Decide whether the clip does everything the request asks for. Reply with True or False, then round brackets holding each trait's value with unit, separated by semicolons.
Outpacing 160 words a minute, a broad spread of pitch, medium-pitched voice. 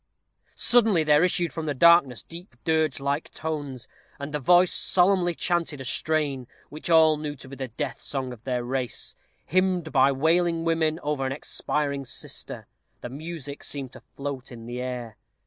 False (170 wpm; 3.8 semitones; 150 Hz)